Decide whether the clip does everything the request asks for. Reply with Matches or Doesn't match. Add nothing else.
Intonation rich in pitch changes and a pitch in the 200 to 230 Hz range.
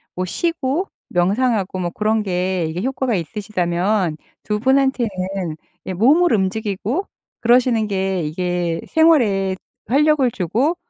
Matches